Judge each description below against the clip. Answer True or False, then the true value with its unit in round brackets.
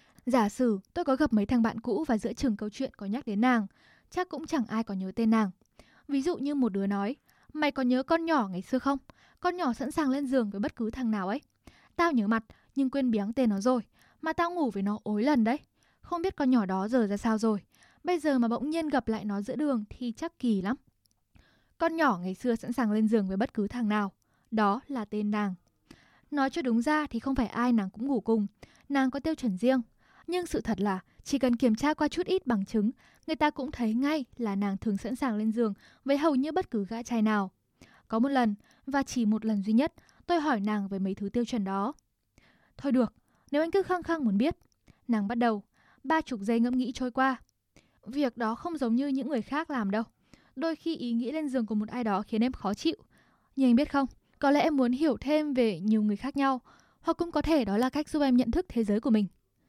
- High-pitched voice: True (245 Hz)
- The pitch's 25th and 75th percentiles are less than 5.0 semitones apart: True (4.6 semitones)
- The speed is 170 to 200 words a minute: False (250 wpm)